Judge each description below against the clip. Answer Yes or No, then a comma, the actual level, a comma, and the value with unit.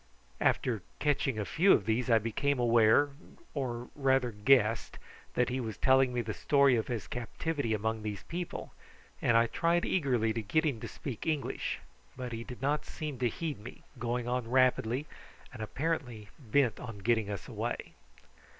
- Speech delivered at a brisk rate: No, average, 170 wpm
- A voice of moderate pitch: No, low, 125 Hz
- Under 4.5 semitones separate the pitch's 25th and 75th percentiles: Yes, average, 3.7 semitones